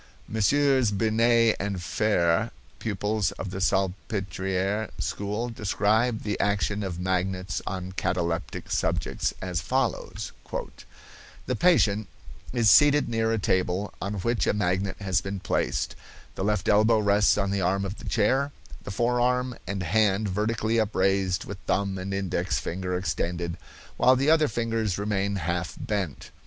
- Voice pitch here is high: No, low, 100 Hz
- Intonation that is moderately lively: Yes, average, 3.1 semitones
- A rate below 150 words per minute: Yes, average, 140 wpm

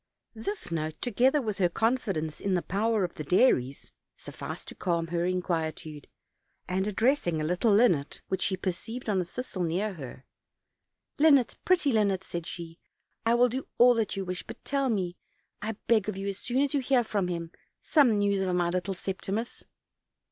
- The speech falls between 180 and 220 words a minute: Yes, average, 185 wpm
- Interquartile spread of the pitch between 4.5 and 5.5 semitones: Yes, average, 5.1 semitones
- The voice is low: No, high, 195 Hz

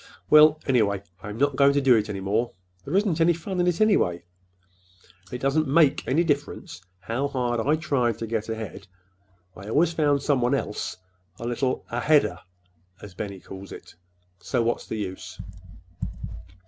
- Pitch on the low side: Yes, low, 130 Hz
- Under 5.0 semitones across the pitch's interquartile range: No, wide, 5.5 semitones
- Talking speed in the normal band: Yes, average, 160 wpm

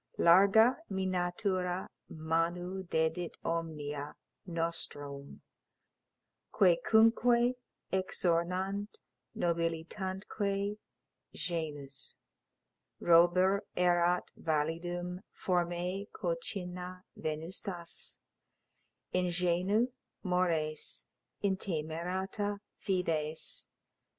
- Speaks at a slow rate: Yes, slow, 50 wpm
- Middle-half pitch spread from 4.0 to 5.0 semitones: No, narrow, 2.5 semitones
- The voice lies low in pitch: No, medium, 180 Hz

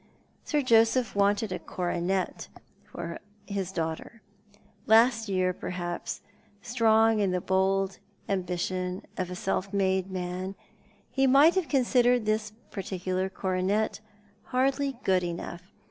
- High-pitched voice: Yes, high, 195 Hz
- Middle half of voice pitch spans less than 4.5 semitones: Yes, average, 3.7 semitones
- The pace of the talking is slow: Yes, slow, 115 wpm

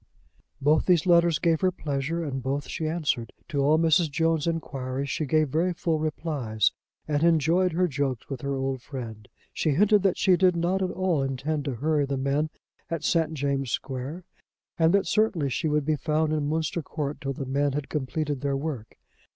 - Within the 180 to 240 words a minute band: Yes, average, 190 wpm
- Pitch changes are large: No, average, 3.3 semitones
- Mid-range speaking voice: Yes, medium, 150 Hz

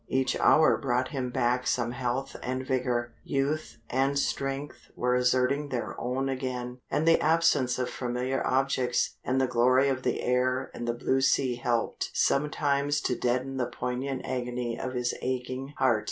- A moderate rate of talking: Yes, average, 165 wpm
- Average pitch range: No, narrow, 1.6 semitones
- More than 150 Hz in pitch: No, low, 130 Hz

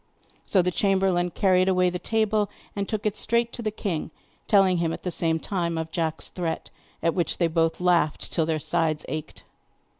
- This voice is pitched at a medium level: Yes, medium, 180 Hz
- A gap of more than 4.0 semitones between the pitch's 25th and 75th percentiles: No, average, 3.1 semitones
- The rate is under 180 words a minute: No, average, 190 wpm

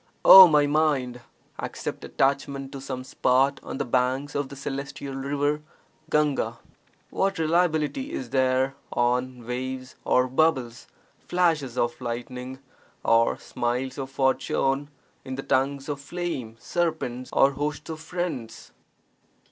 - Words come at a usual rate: No, slow, 125 wpm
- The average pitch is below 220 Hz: Yes, low, 135 Hz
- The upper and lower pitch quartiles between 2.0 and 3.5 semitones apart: Yes, narrow, 2.6 semitones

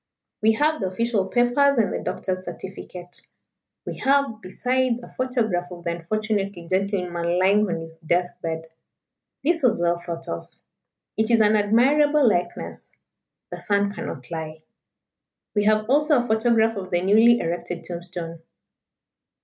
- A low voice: No, high, 205 Hz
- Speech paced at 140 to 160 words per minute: Yes, average, 145 wpm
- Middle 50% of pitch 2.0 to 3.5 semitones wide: No, average, 5.2 semitones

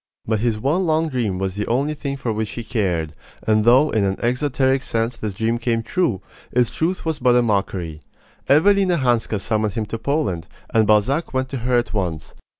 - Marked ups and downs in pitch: No, average, 4.4 semitones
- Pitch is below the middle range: Yes, low, 120 Hz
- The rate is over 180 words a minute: Yes, average, 200 wpm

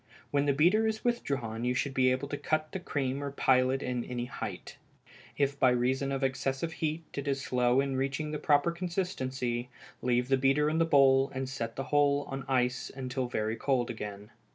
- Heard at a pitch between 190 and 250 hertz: No, low, 135 Hz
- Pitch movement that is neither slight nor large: No, narrow, 2.3 semitones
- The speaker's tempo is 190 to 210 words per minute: Yes, average, 200 wpm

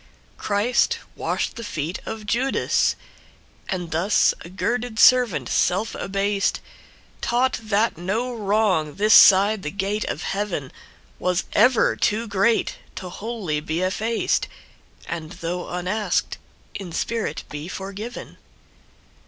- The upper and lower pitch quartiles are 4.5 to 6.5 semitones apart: No, average, 3.8 semitones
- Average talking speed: No, slow, 105 wpm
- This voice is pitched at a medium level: No, high, 200 Hz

